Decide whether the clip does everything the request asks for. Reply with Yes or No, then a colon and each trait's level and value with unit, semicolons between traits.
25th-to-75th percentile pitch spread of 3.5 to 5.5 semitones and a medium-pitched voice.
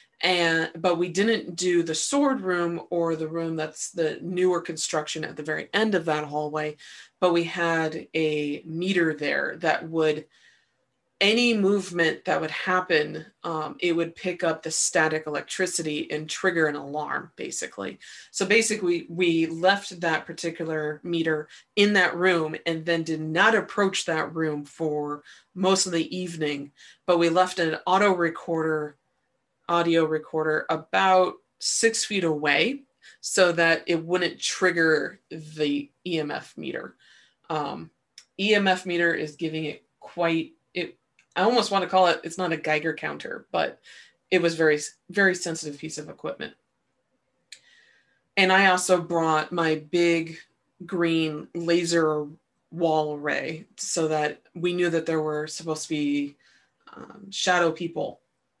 No: narrow, 2.6 semitones; medium, 165 Hz